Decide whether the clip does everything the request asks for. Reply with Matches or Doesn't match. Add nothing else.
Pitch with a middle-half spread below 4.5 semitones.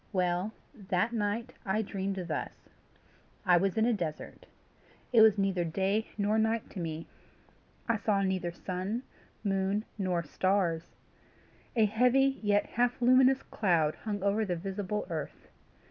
Matches